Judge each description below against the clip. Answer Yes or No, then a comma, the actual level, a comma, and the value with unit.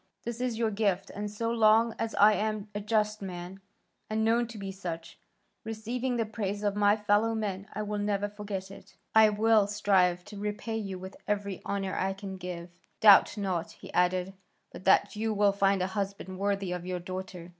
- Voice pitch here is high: Yes, high, 205 Hz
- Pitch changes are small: Yes, narrow, 2.1 semitones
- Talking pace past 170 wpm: Yes, average, 195 wpm